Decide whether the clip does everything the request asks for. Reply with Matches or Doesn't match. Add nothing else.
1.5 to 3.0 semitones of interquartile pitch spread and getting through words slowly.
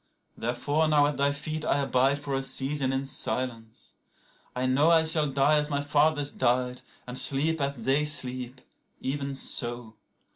Doesn't match